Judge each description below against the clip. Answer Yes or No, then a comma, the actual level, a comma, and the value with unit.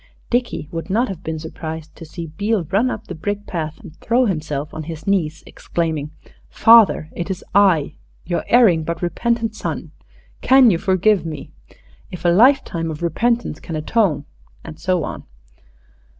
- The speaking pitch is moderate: Yes, medium, 175 Hz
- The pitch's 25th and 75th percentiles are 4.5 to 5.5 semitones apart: Yes, average, 5.2 semitones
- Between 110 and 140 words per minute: No, average, 165 wpm